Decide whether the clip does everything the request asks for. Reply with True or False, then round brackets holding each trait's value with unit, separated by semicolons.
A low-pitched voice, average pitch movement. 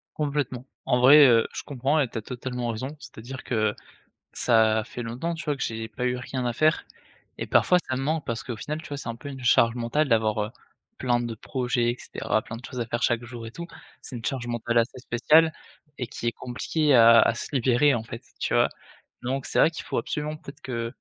True (125 Hz; 3.1 semitones)